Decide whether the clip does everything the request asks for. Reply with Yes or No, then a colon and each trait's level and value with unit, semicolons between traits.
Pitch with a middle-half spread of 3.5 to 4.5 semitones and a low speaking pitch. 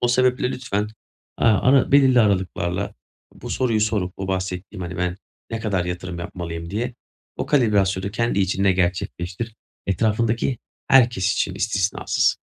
Yes: average, 4.1 semitones; low, 100 Hz